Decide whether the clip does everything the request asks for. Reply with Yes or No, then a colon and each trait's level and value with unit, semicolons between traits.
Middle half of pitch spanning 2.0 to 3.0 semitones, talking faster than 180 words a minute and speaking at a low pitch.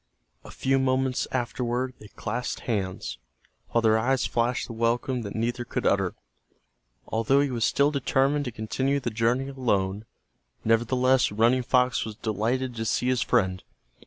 No: narrow, 2.6 semitones; average, 155 wpm; low, 120 Hz